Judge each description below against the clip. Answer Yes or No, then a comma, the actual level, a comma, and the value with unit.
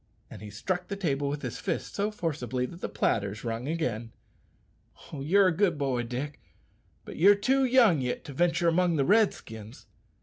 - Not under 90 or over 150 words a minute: No, average, 175 wpm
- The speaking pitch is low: No, medium, 155 Hz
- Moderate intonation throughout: No, wide, 6.9 semitones